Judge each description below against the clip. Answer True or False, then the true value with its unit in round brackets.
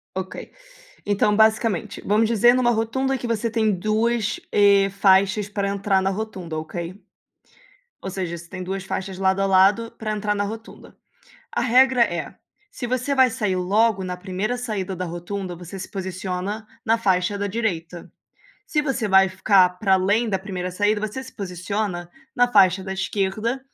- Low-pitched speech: False (200 Hz)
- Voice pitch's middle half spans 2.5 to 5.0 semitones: True (2.8 semitones)